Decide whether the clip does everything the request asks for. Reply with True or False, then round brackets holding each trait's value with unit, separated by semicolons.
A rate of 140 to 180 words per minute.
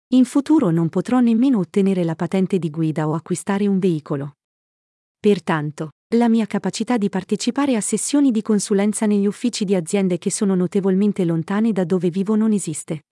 True (170 wpm)